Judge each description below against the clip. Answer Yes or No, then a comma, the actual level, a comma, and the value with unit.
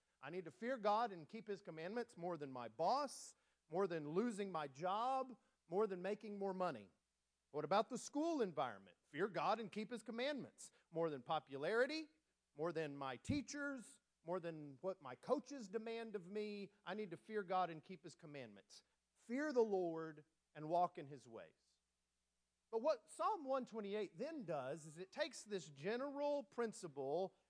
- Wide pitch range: Yes, wide, 6.8 semitones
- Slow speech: No, average, 170 wpm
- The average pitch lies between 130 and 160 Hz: No, high, 190 Hz